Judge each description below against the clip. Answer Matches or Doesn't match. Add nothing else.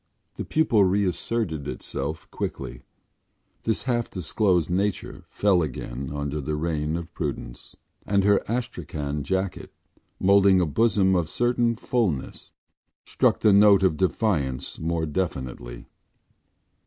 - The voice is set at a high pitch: Doesn't match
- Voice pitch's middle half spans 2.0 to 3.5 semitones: Doesn't match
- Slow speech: Matches